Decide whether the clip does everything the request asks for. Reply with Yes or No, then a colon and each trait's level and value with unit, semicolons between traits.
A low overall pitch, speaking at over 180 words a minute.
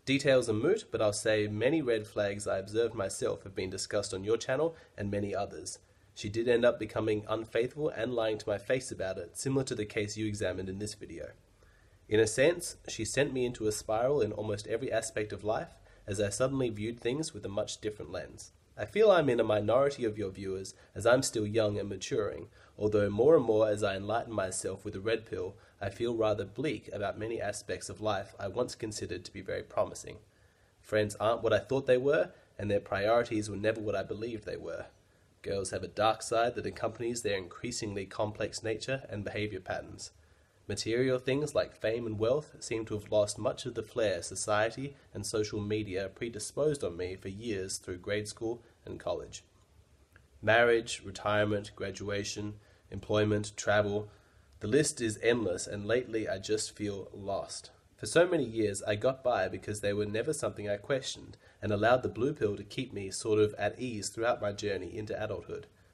Yes: low, 105 Hz; average, 195 wpm